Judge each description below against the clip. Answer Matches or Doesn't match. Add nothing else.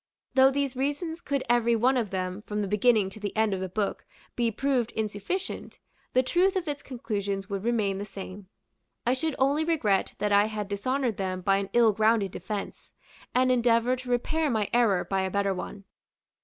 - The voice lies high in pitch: Matches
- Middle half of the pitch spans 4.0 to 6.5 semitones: Matches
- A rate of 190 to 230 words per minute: Matches